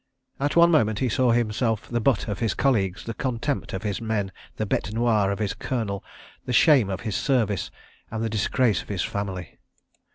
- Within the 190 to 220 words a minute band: Yes, average, 195 wpm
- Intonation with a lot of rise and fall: No, average, 3.4 semitones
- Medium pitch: No, low, 110 Hz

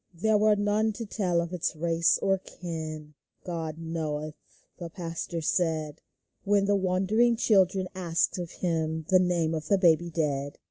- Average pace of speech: Yes, average, 165 wpm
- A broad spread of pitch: No, average, 3.1 semitones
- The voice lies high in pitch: No, medium, 170 Hz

